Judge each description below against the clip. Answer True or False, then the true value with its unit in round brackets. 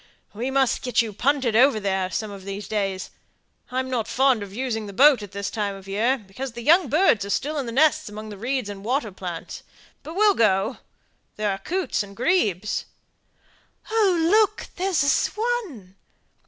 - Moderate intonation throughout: False (5.9 semitones)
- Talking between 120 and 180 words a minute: False (190 wpm)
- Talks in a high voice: True (235 Hz)